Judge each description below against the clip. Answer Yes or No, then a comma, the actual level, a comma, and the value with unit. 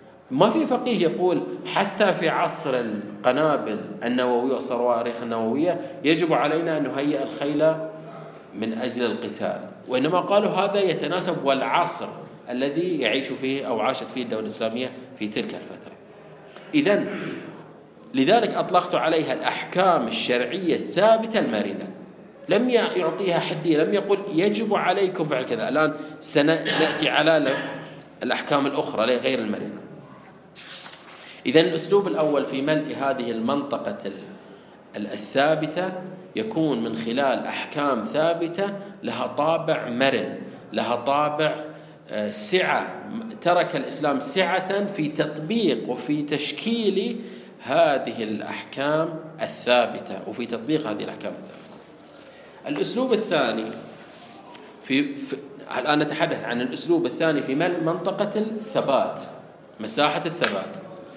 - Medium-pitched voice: Yes, medium, 160 Hz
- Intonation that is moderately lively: No, wide, 5.8 semitones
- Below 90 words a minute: No, average, 105 wpm